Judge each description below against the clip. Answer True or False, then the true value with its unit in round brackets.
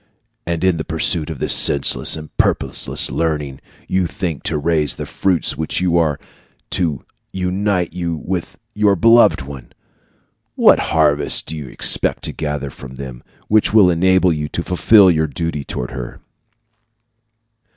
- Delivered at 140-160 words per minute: True (150 wpm)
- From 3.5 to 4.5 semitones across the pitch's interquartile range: True (3.9 semitones)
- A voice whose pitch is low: True (80 Hz)